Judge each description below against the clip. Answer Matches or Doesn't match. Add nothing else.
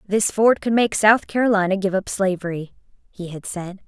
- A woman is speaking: Matches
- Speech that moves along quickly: Doesn't match